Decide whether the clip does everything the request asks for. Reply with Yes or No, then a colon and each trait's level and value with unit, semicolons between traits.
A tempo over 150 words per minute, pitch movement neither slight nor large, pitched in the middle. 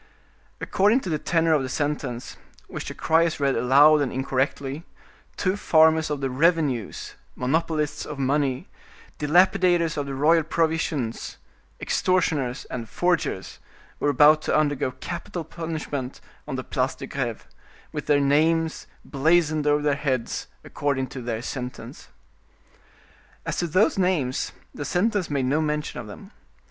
No: average, 140 wpm; average, 3.4 semitones; medium, 150 Hz